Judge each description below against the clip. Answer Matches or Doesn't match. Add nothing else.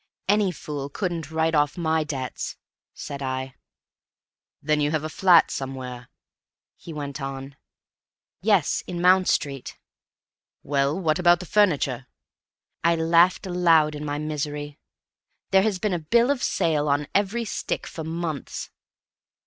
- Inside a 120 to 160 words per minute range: Matches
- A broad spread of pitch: Doesn't match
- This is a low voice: Doesn't match